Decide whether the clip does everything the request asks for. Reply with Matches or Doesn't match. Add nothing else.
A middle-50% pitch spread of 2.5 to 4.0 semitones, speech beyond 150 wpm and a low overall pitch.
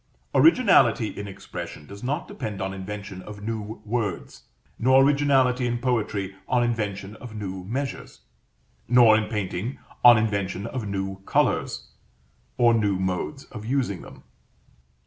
Doesn't match